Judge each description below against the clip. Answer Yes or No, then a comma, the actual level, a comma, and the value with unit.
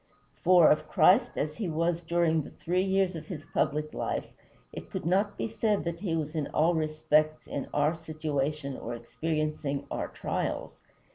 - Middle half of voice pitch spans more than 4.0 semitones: No, narrow, 2.4 semitones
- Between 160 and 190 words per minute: Yes, average, 170 wpm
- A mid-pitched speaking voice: Yes, medium, 160 Hz